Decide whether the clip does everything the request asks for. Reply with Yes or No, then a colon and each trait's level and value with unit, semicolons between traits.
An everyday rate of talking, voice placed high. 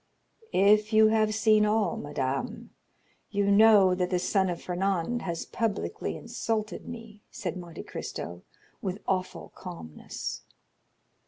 No: slow, 120 wpm; high, 200 Hz